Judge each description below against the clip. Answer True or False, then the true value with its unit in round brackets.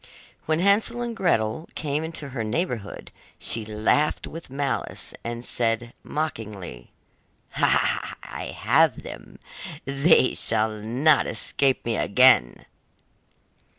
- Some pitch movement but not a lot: False (6.1 semitones)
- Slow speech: True (105 wpm)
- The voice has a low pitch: True (130 Hz)